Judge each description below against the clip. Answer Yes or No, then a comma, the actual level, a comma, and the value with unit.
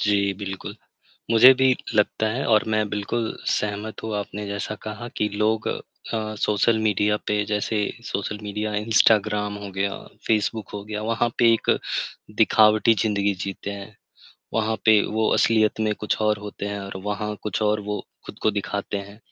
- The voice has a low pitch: Yes, low, 105 Hz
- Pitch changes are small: Yes, narrow, 1.2 semitones